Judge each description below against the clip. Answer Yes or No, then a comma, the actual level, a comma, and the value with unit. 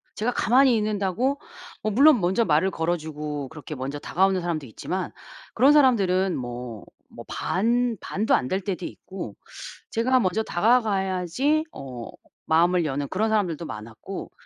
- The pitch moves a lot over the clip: Yes, wide, 6.5 semitones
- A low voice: No, medium, 185 Hz